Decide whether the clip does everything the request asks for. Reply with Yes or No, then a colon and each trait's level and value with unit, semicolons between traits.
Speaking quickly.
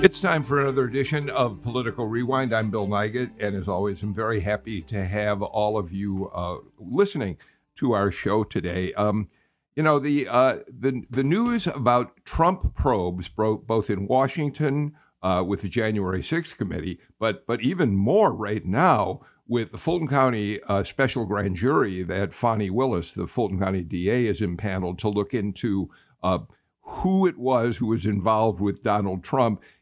No: average, 170 wpm